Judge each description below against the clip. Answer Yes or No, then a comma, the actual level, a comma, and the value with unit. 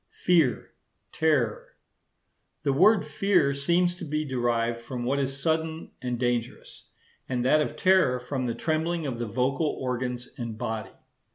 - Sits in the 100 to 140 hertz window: Yes, low, 135 Hz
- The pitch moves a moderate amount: Yes, average, 4.6 semitones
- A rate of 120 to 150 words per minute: Yes, average, 145 wpm